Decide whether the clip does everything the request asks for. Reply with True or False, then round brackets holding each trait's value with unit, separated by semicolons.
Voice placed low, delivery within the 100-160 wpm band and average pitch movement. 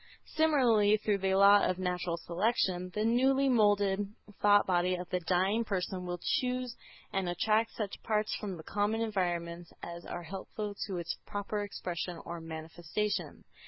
False (195 Hz; 155 wpm; 3.3 semitones)